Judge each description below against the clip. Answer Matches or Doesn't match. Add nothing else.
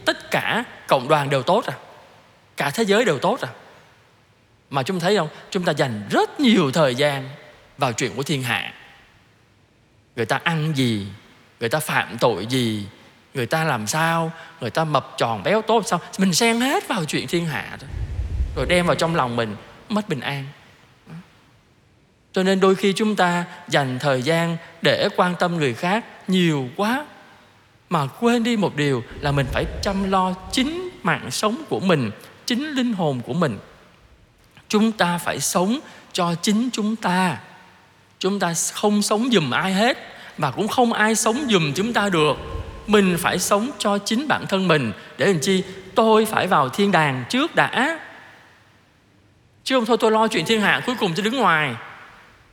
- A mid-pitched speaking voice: Matches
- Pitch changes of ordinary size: Doesn't match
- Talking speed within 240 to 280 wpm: Doesn't match